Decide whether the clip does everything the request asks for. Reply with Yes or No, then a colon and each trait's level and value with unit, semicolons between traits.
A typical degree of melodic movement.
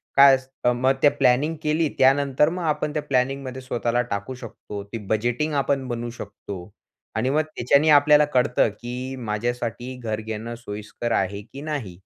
Yes: average, 3.3 semitones